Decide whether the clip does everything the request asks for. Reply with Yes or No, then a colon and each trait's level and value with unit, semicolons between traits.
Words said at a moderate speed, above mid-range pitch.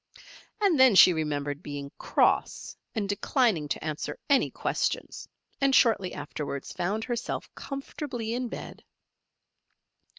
No: slow, 120 wpm; high, 210 Hz